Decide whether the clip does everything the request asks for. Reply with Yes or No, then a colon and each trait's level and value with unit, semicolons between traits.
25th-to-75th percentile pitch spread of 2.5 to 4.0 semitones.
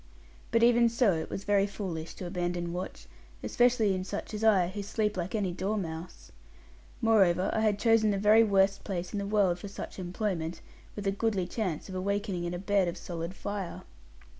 Yes: average, 3.0 semitones